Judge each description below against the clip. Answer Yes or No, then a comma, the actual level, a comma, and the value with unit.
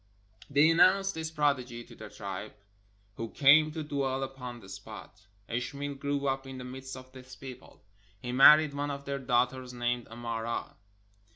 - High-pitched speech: No, low, 130 Hz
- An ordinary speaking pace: Yes, average, 165 wpm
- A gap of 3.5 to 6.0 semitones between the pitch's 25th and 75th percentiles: No, average, 2.7 semitones